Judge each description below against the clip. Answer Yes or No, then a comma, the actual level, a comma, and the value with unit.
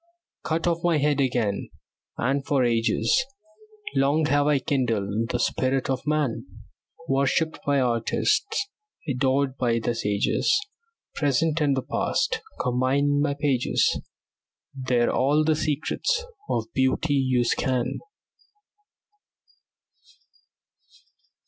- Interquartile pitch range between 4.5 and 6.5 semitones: No, average, 3.1 semitones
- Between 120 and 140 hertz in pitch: Yes, low, 135 Hz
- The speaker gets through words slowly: Yes, slow, 105 wpm